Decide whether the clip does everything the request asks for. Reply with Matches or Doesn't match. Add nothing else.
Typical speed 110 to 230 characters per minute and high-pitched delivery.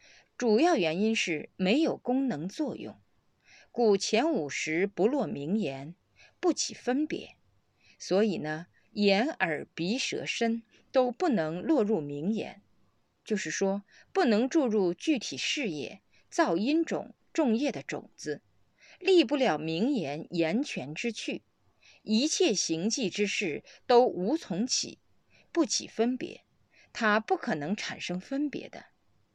Matches